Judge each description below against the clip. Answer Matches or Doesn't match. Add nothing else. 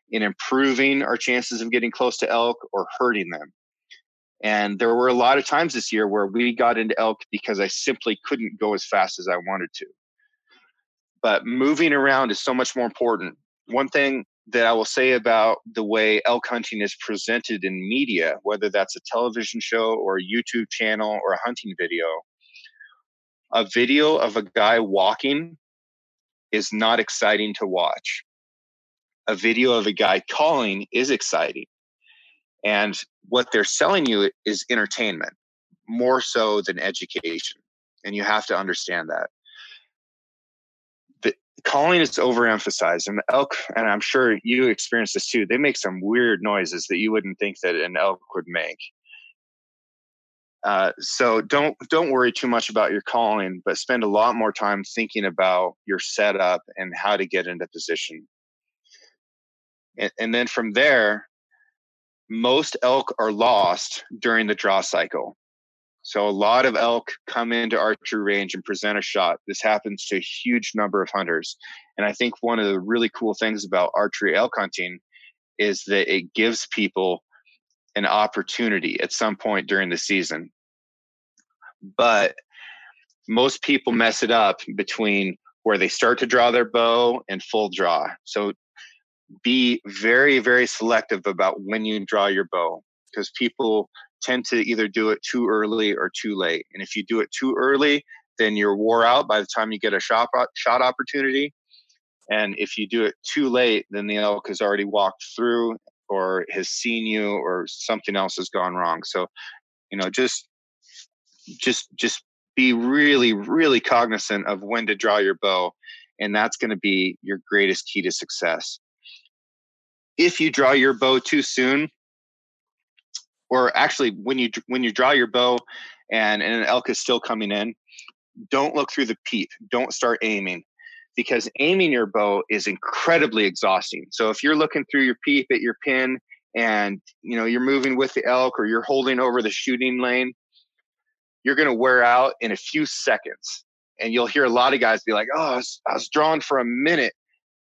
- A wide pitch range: Doesn't match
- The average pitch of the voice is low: Matches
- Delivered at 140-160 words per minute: Doesn't match